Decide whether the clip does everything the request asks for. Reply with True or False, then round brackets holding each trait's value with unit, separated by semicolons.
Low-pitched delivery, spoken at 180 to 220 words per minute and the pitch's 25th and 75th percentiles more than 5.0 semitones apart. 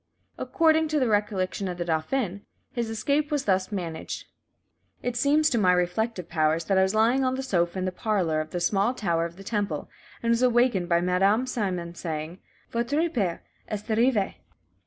False (200 Hz; 185 wpm; 5.6 semitones)